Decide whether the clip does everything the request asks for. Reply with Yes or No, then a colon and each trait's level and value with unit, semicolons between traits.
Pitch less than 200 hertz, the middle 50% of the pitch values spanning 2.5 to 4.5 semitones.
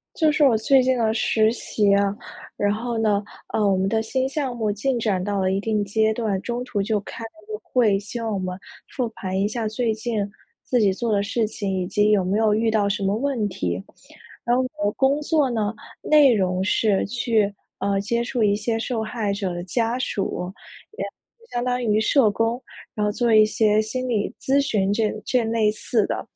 No: high, 220 Hz; average, 2.9 semitones